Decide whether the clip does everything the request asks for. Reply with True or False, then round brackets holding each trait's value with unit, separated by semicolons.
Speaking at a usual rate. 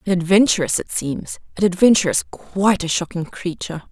True (155 wpm)